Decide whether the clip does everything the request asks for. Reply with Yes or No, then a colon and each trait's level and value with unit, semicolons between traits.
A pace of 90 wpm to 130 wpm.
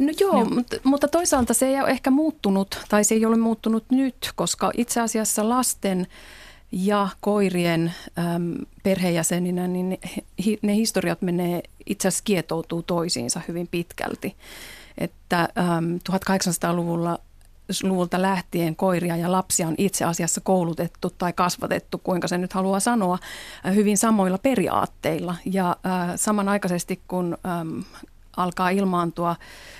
Yes: average, 115 wpm